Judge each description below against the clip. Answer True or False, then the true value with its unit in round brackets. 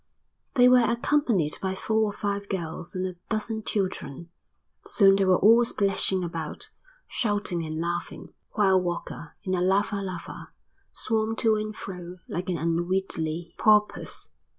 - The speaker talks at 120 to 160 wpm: True (145 wpm)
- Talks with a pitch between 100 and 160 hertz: False (190 Hz)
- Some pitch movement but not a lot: True (3.6 semitones)